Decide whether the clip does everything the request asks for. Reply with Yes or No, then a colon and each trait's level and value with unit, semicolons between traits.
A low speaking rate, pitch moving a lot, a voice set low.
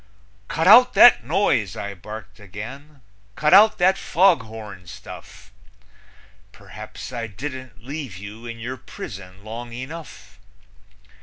Yes: slow, 120 wpm; wide, 6.6 semitones; low, 120 Hz